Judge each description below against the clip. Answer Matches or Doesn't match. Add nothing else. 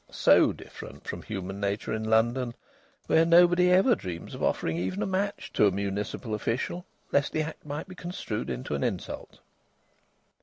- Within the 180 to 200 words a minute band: Doesn't match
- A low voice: Matches